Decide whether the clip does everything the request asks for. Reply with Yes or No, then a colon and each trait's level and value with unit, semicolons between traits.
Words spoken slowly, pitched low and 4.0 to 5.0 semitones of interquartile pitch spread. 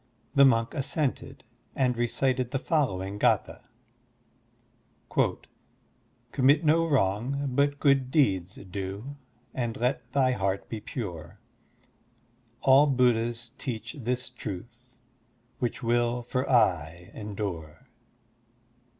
Yes: slow, 100 wpm; low, 120 Hz; average, 4.6 semitones